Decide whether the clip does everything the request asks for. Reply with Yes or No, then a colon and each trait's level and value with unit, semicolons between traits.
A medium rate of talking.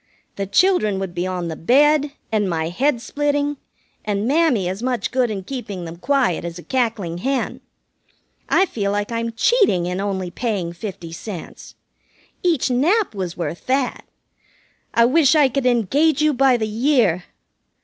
Yes: average, 160 wpm